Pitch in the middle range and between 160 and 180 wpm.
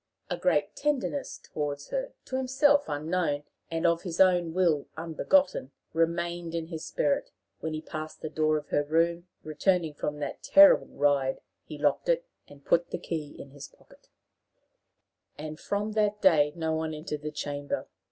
Yes: medium, 160 Hz; average, 165 wpm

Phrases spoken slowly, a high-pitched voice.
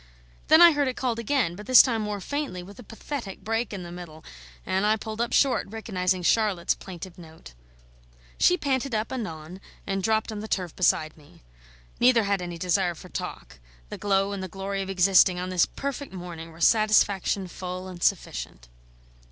No: average, 185 wpm; high, 195 Hz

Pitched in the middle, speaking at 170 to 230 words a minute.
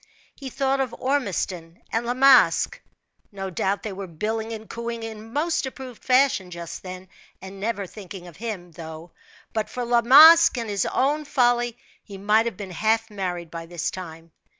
No: high, 215 Hz; average, 175 wpm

